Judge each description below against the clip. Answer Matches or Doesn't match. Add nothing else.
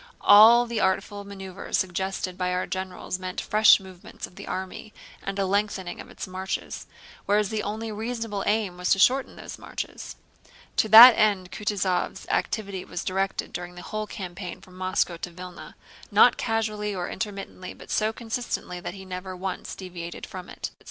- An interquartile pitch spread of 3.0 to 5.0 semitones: Doesn't match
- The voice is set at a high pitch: Matches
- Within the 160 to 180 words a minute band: Matches